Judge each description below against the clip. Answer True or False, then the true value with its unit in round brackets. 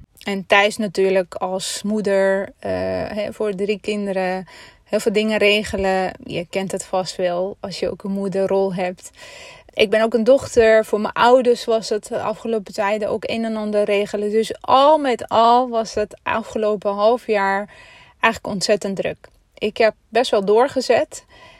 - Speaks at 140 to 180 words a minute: True (165 wpm)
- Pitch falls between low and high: False (210 Hz)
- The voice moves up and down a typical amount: False (2.3 semitones)